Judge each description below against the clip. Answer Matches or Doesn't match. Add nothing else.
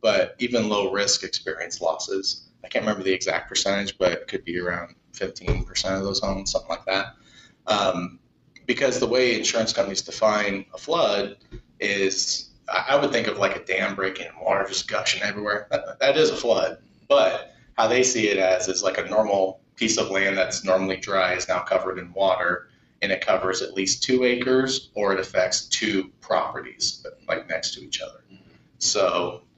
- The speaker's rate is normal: Matches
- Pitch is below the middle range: Matches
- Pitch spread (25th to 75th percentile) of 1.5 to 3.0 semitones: Matches